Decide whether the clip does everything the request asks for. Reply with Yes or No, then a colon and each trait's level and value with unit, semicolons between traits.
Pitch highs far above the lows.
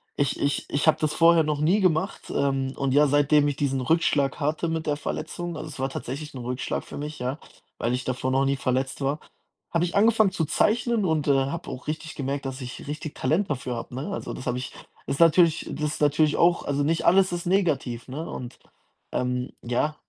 No: average, 3.4 semitones